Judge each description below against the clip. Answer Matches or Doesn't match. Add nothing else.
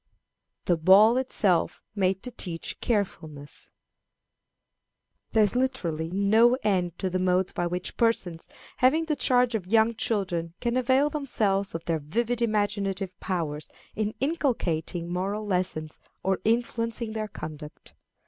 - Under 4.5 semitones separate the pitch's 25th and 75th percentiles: Doesn't match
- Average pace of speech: Doesn't match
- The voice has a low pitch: Doesn't match